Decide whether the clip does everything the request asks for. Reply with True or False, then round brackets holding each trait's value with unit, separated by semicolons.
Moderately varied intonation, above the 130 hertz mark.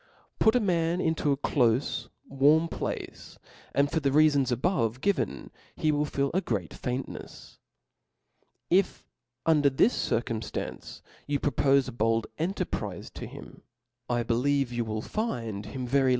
True (4.9 semitones; 140 Hz)